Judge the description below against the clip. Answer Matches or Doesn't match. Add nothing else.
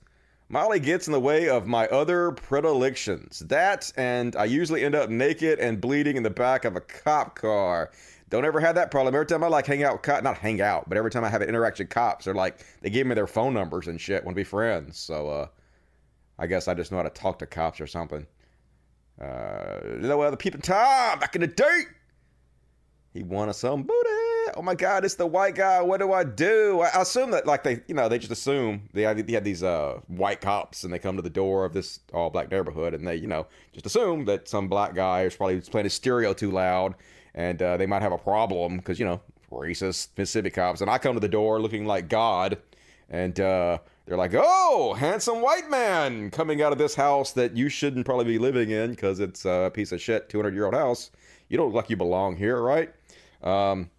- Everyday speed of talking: Doesn't match